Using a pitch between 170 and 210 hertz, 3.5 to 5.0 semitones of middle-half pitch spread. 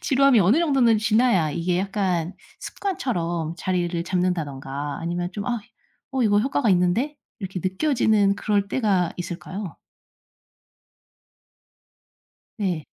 Yes: high, 190 Hz; average, 4.7 semitones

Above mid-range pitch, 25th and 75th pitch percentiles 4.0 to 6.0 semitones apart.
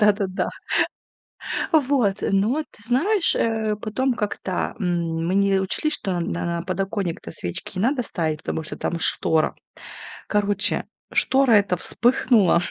Yes: high, 200 Hz; average, 4.8 semitones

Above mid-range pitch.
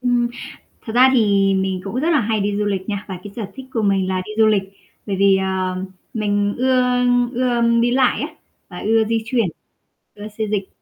Yes: high, 210 Hz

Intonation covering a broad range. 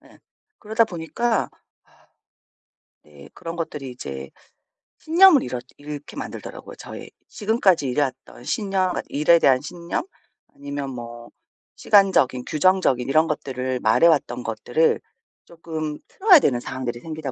Yes: wide, 6.5 semitones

